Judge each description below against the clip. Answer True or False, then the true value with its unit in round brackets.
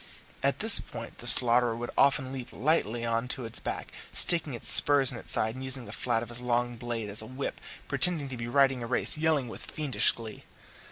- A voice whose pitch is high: False (125 Hz)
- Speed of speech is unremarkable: False (220 wpm)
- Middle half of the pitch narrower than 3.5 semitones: True (2.7 semitones)